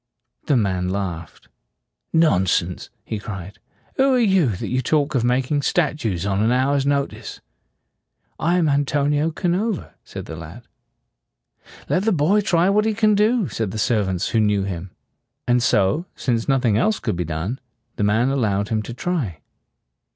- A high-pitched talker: No, low, 125 Hz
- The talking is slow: No, average, 165 wpm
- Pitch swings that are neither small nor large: No, wide, 8.4 semitones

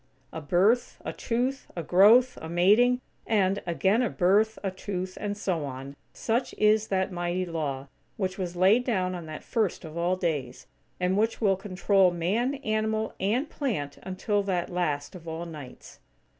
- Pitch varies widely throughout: No, average, 4.0 semitones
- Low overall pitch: No, high, 190 Hz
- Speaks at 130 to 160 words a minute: No, average, 170 wpm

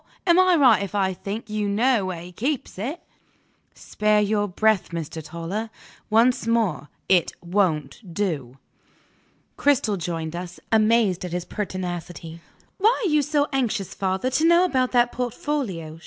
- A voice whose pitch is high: Yes, high, 205 Hz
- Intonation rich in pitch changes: Yes, wide, 6.0 semitones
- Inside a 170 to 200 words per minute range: No, average, 150 wpm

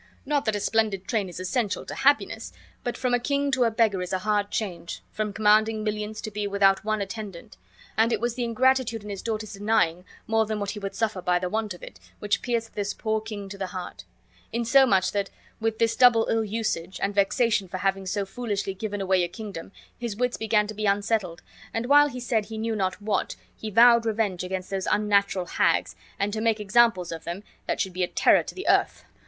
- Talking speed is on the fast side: Yes, fast, 225 wpm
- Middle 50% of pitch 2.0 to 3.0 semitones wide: Yes, narrow, 2.6 semitones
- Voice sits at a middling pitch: No, high, 210 Hz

